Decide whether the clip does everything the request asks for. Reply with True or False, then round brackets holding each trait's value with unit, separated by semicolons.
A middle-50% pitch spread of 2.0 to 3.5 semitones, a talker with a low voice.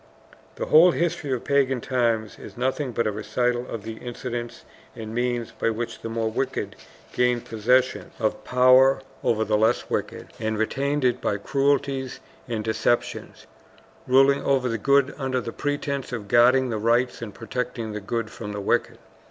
True (2.8 semitones; 120 Hz)